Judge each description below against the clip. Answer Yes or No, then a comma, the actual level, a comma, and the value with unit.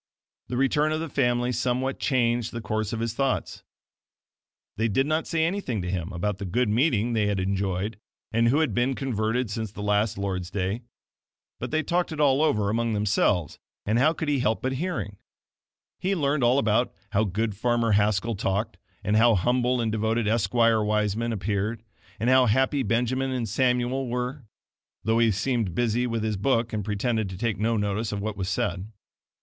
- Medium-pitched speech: No, low, 115 Hz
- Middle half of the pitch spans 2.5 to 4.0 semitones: Yes, average, 3.4 semitones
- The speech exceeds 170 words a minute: Yes, average, 190 wpm